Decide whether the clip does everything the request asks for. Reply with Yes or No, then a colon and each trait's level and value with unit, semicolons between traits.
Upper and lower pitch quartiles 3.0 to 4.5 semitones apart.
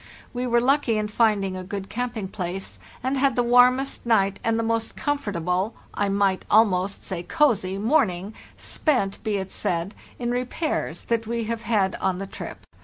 Yes: average, 4.0 semitones